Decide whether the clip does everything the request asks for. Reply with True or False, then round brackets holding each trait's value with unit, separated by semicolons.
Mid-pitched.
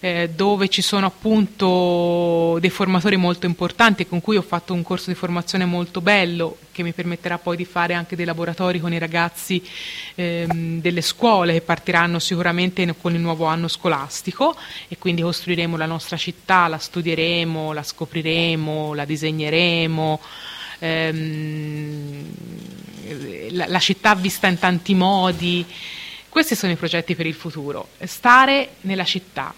True (175 Hz)